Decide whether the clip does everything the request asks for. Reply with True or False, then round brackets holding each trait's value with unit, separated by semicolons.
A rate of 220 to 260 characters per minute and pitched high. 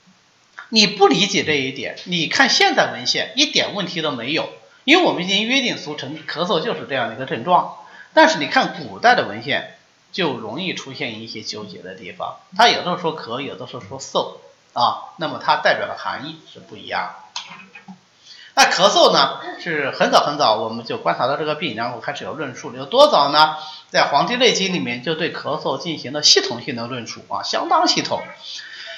False (295 characters per minute; 200 Hz)